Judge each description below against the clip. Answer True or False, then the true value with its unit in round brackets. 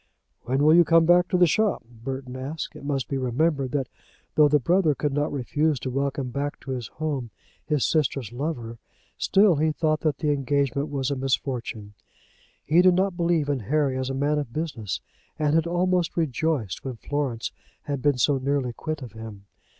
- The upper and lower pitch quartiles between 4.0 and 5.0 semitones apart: False (3.3 semitones)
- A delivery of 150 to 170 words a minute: False (190 wpm)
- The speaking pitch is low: False (145 Hz)